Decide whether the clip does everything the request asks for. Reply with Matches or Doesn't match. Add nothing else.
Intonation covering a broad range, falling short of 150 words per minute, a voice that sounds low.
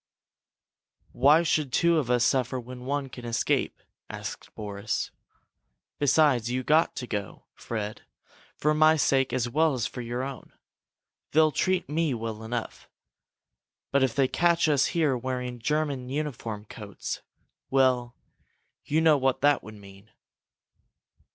Doesn't match